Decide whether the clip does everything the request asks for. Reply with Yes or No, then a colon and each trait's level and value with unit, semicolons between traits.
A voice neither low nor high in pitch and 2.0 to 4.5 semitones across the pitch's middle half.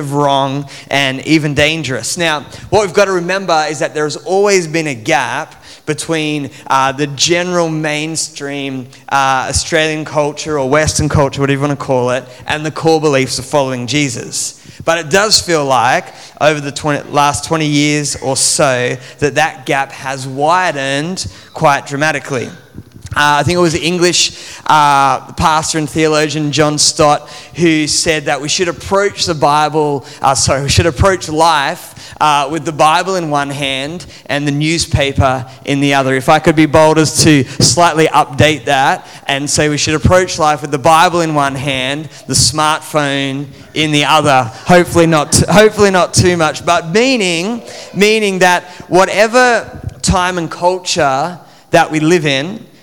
Yes: medium, 150 Hz; average, 3.1 semitones